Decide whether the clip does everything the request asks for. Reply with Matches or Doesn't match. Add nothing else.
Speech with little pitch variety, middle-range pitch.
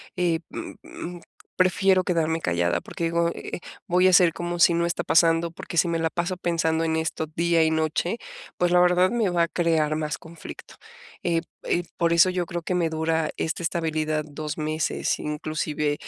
Matches